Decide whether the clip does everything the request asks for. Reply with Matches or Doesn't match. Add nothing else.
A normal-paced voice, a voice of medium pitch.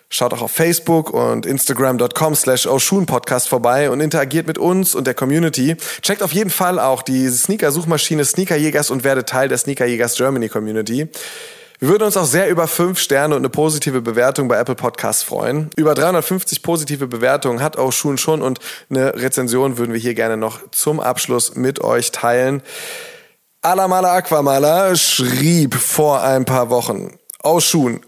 Matches